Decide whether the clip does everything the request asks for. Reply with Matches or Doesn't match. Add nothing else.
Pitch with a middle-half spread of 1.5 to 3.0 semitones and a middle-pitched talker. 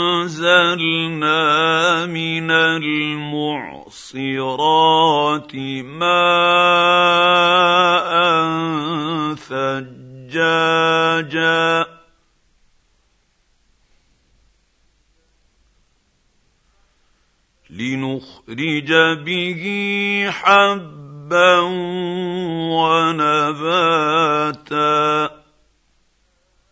Matches